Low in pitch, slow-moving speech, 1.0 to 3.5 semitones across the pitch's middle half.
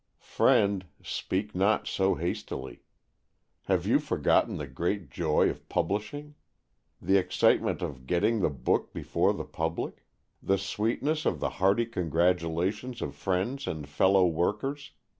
No: very low, 95 Hz; slow, 130 wpm; average, 4.2 semitones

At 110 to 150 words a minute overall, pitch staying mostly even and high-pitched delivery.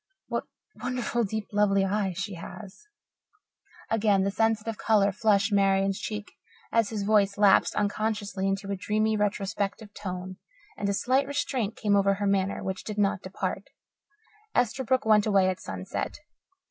Yes: average, 145 wpm; narrow, 1.8 semitones; high, 205 Hz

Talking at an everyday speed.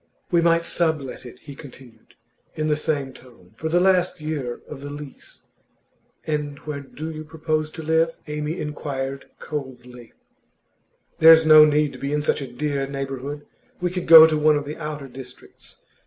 Yes: average, 170 wpm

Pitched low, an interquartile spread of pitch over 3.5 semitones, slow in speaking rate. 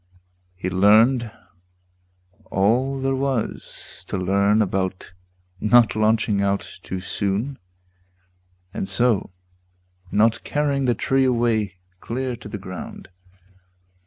Yes: low, 110 Hz; average, 4.2 semitones; slow, 100 wpm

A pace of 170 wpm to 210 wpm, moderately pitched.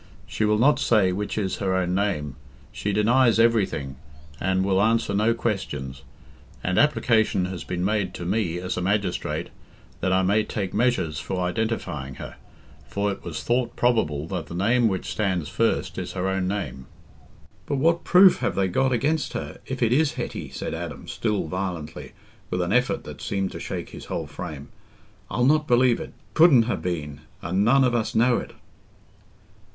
No: average, 180 wpm; low, 100 Hz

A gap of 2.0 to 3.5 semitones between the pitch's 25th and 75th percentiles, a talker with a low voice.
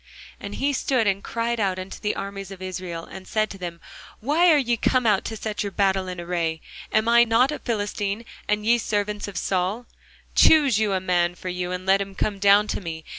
No: average, 3.2 semitones; high, 200 Hz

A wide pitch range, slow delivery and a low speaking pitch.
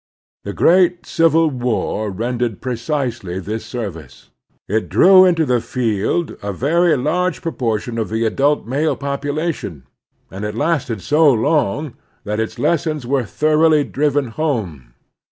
Yes: wide, 5.8 semitones; slow, 130 wpm; low, 130 Hz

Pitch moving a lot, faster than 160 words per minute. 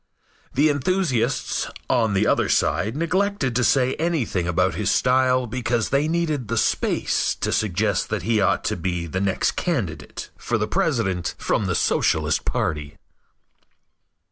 No: wide, 6.6 semitones; average, 140 wpm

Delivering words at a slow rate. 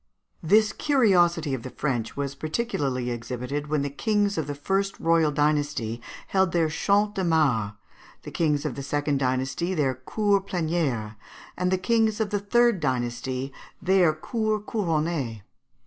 No: average, 155 wpm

